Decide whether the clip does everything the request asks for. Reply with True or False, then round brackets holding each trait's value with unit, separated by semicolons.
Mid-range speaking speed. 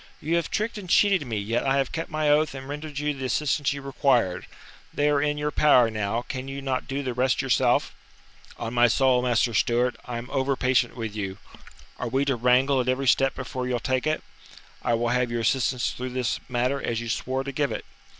False (225 wpm)